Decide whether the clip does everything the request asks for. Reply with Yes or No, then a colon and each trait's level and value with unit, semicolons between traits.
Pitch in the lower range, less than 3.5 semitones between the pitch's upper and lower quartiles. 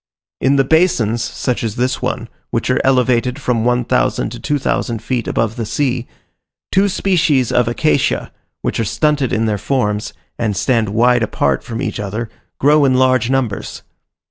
Yes: low, 125 Hz; average, 2.8 semitones